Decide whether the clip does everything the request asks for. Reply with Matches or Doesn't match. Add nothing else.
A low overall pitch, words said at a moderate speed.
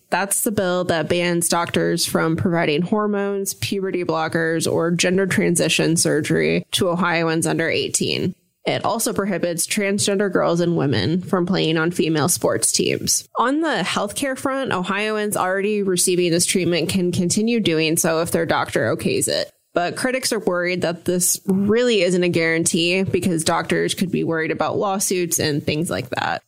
Doesn't match